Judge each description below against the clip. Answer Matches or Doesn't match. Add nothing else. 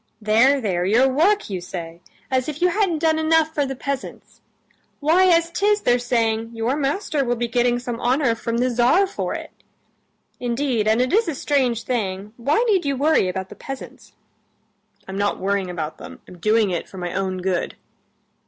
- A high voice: Matches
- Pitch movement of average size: Doesn't match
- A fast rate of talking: Doesn't match